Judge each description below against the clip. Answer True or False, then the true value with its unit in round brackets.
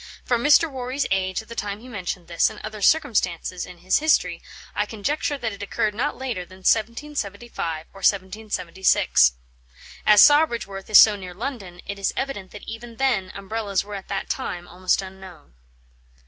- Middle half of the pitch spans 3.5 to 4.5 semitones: True (4.1 semitones)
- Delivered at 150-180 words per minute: True (170 wpm)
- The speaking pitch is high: True (205 Hz)